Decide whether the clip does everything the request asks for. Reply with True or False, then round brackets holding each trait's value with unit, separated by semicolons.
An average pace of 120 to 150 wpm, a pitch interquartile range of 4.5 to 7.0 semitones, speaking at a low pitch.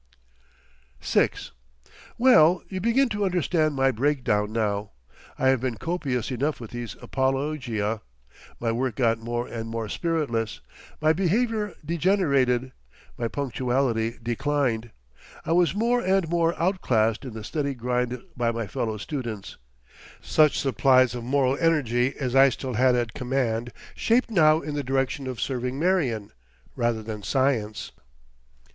True (140 wpm; 4.9 semitones; 130 Hz)